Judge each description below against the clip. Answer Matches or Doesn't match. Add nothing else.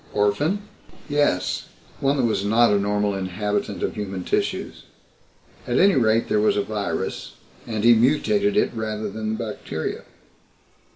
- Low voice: Matches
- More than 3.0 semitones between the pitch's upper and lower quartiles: Matches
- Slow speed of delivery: Doesn't match